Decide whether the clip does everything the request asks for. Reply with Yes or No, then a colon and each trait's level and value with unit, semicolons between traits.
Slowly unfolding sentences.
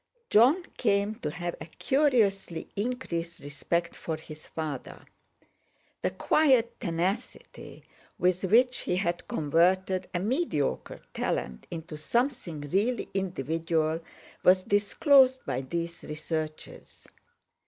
Yes: slow, 105 wpm